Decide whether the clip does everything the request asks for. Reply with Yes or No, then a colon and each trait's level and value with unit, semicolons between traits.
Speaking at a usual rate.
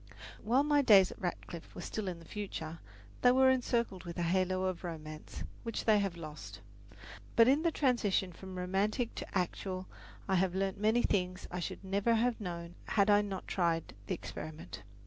Yes: average, 185 wpm